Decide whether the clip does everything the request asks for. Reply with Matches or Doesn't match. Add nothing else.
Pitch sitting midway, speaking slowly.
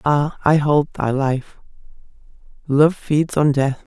Matches